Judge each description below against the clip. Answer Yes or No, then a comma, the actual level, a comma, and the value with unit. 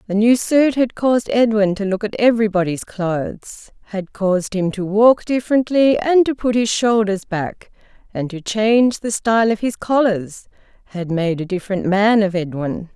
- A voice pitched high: Yes, high, 210 Hz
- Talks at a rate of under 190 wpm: Yes, average, 175 wpm